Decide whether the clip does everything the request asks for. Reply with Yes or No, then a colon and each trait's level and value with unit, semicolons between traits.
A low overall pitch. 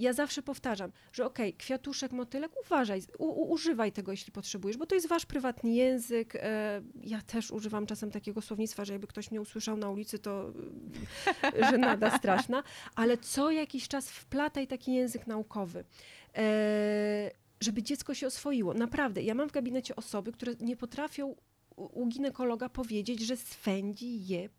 No: high, 235 Hz